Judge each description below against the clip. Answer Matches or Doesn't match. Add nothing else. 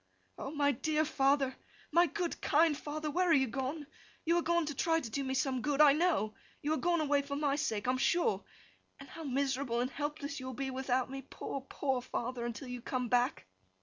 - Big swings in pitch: Doesn't match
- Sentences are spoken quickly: Matches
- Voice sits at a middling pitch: Doesn't match